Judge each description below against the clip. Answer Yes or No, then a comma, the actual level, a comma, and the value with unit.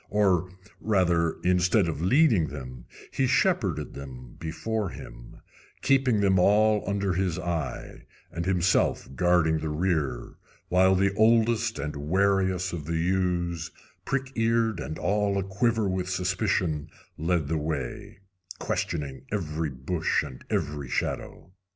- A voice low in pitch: Yes, very low, 90 Hz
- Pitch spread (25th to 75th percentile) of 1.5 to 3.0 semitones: No, average, 4.3 semitones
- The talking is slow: Yes, slow, 130 wpm